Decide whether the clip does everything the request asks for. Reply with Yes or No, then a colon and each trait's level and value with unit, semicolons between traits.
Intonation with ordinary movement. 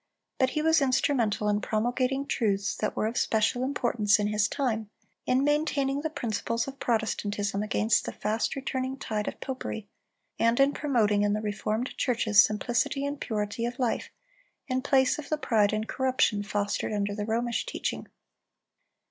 Yes: average, 4.0 semitones